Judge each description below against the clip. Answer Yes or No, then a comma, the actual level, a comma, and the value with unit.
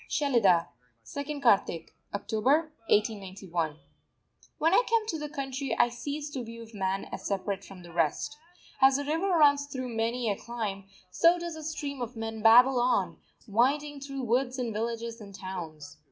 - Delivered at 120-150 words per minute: No, average, 165 wpm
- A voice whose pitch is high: Yes, high, 240 Hz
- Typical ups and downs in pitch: No, wide, 5.9 semitones